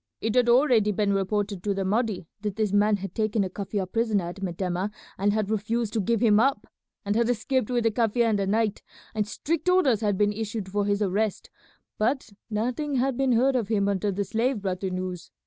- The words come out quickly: Yes, fast, 215 wpm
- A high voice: Yes, high, 210 Hz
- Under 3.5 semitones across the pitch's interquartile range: Yes, average, 2.8 semitones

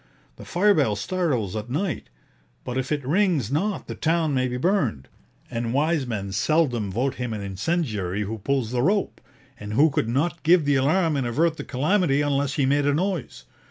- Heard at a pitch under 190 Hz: Yes, medium, 140 Hz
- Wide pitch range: Yes, wide, 6.0 semitones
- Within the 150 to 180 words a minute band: No, average, 195 wpm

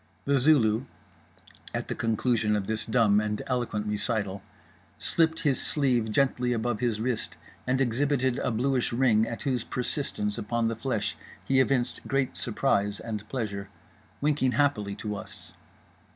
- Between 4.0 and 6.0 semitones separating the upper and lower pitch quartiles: No, average, 3.6 semitones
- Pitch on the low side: Yes, low, 120 Hz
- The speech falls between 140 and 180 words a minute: Yes, average, 145 wpm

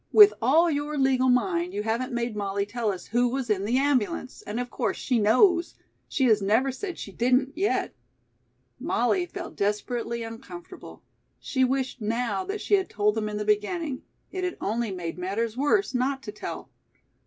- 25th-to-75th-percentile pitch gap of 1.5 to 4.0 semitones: No, average, 5.3 semitones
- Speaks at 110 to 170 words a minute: No, average, 180 wpm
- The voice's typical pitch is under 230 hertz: No, high, 245 Hz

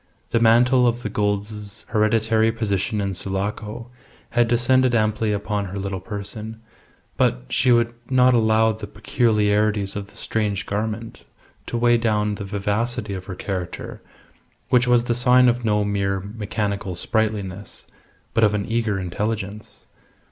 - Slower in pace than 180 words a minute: Yes, average, 145 wpm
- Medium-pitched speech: No, low, 105 Hz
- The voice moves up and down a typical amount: No, narrow, 2.3 semitones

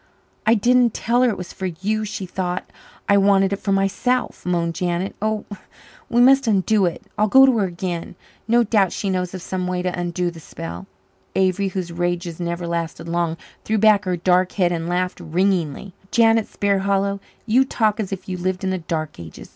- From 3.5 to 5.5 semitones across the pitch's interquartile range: No, average, 3.1 semitones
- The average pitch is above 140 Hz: Yes, medium, 185 Hz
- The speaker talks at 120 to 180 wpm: No, average, 200 wpm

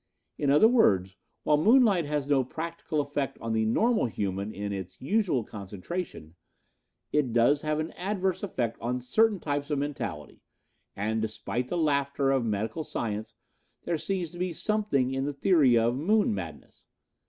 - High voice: No, medium, 140 Hz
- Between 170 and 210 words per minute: No, average, 160 wpm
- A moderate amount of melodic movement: No, wide, 7.1 semitones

